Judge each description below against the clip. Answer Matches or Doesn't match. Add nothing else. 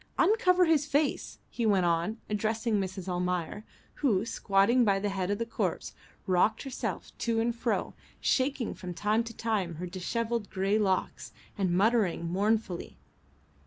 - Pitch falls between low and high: Doesn't match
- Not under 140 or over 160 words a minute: Matches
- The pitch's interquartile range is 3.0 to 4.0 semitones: Matches